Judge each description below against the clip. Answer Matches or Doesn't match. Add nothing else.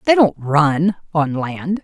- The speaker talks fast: Doesn't match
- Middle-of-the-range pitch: Matches